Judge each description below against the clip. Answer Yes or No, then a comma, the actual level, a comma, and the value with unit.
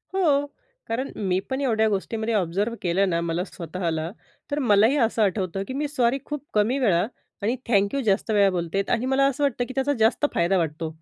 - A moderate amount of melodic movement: No, wide, 6.2 semitones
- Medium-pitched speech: No, high, 220 Hz